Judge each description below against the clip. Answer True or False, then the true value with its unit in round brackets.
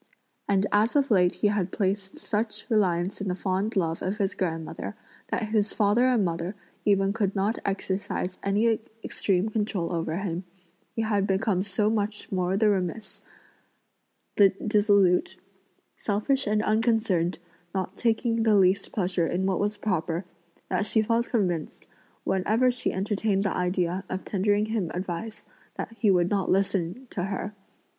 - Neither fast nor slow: True (150 wpm)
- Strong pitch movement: False (2.7 semitones)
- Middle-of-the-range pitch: False (200 Hz)